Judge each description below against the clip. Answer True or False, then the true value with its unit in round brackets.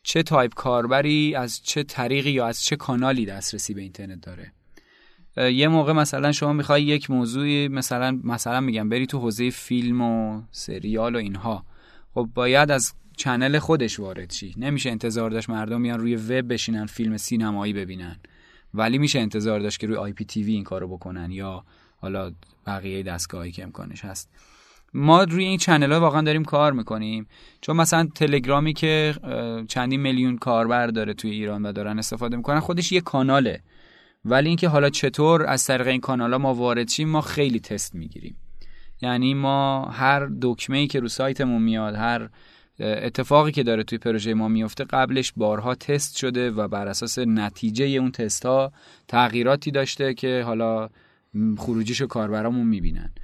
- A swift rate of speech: True (160 wpm)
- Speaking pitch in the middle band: False (120 Hz)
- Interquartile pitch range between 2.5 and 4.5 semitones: True (4.2 semitones)